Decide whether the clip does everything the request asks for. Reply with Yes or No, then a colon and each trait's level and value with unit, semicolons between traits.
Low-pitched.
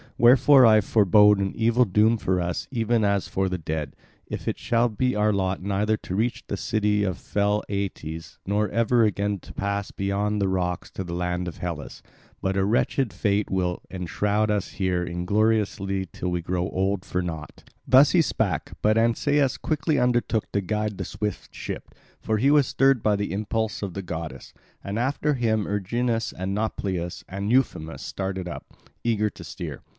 Yes: low, 100 Hz